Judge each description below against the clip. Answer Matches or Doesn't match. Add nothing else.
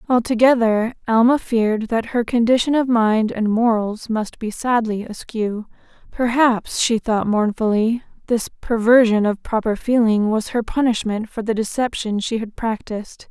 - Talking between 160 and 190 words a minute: Doesn't match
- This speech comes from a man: Doesn't match